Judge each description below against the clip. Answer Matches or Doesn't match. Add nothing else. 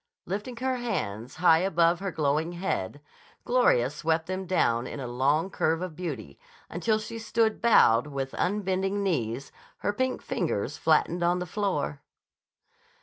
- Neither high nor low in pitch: Matches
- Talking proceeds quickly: Doesn't match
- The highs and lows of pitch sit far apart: Matches